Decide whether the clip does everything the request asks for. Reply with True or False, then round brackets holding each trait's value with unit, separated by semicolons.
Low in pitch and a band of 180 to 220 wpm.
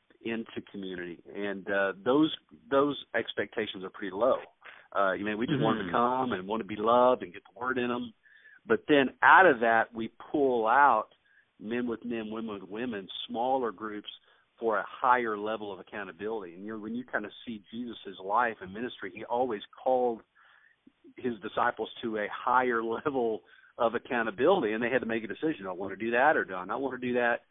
True (115 Hz; 205 wpm)